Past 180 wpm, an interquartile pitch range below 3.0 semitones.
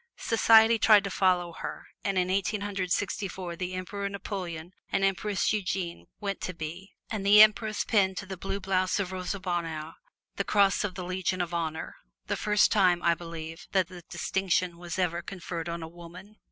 Yes: average, 190 wpm; narrow, 2.4 semitones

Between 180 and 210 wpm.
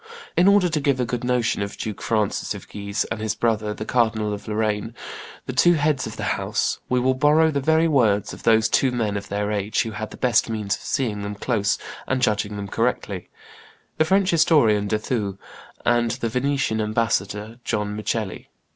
Yes: average, 200 wpm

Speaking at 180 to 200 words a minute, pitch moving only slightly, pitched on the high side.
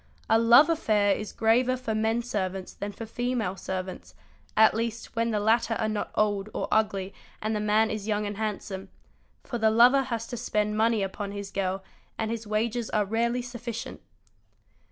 Yes: average, 185 wpm; narrow, 2.1 semitones; high, 220 Hz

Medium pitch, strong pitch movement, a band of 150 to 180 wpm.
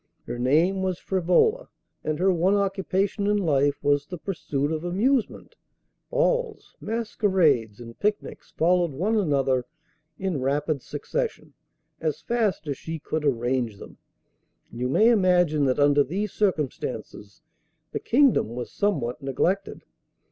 No: medium, 170 Hz; wide, 6.2 semitones; slow, 135 wpm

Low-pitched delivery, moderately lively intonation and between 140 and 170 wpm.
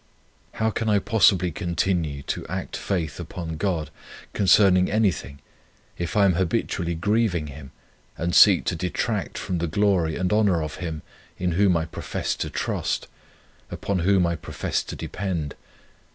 Yes: very low, 90 Hz; average, 3.4 semitones; average, 150 wpm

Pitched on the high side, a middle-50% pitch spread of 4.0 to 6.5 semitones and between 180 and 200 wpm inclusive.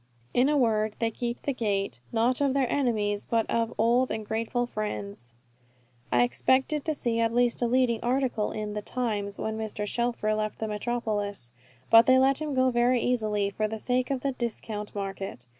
No: high, 230 Hz; average, 3.0 semitones; average, 190 wpm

